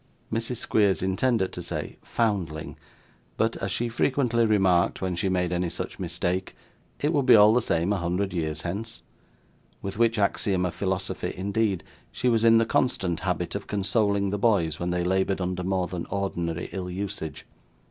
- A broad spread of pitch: No, average, 3.8 semitones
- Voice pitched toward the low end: Yes, very low, 95 Hz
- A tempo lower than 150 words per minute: No, average, 175 wpm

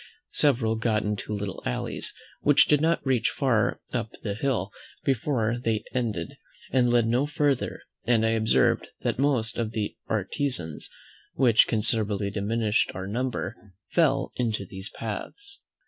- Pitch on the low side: Yes, low, 115 Hz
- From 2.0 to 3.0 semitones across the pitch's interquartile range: No, average, 3.8 semitones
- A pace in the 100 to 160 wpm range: Yes, average, 140 wpm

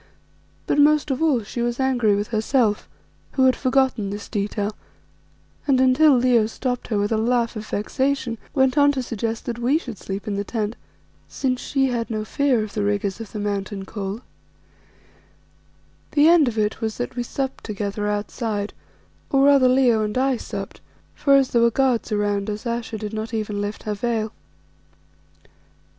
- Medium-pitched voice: No, high, 230 Hz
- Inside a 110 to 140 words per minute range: No, average, 180 wpm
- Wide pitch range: No, average, 3.8 semitones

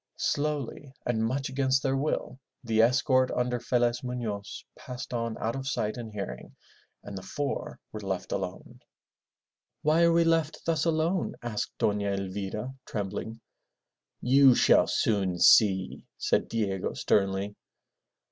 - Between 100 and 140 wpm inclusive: Yes, slow, 135 wpm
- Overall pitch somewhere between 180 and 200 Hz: No, low, 120 Hz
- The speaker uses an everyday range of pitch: Yes, average, 4.8 semitones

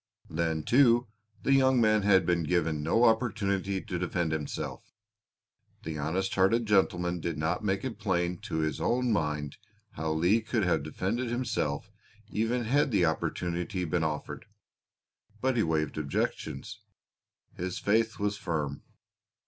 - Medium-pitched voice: No, very low, 95 Hz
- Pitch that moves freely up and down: Yes, wide, 5.7 semitones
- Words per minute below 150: Yes, average, 140 wpm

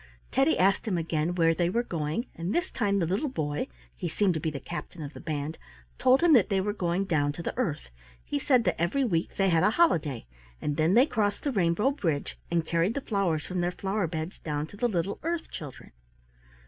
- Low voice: No, medium, 180 Hz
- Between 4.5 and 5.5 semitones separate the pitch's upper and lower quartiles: Yes, average, 5.0 semitones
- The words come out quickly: Yes, fast, 225 wpm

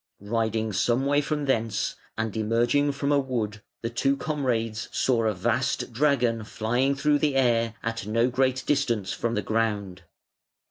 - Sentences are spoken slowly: No, average, 155 wpm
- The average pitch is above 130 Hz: No, low, 120 Hz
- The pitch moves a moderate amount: Yes, average, 3.5 semitones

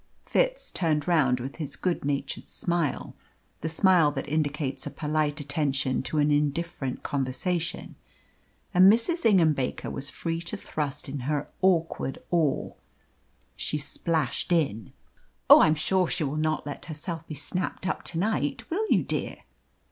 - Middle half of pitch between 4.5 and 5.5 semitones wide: No, average, 3.3 semitones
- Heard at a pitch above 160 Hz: No, medium, 155 Hz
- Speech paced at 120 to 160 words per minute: Yes, average, 155 wpm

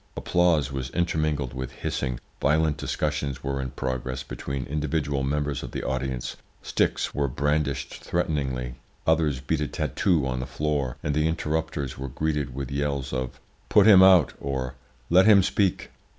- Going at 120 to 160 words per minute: Yes, average, 155 wpm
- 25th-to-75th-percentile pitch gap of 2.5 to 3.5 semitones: Yes, average, 2.9 semitones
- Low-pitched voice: Yes, very low, 70 Hz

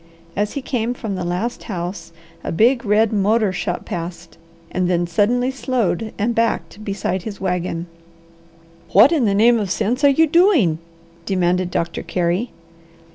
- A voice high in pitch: Yes, high, 205 Hz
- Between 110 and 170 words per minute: Yes, average, 155 wpm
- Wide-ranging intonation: No, average, 4.9 semitones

